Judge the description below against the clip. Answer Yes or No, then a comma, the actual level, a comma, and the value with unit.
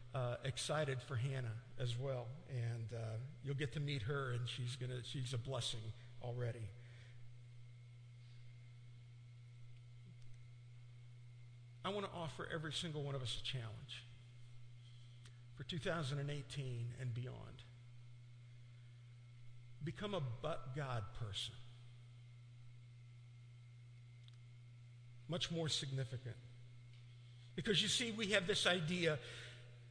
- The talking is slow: Yes, slow, 100 wpm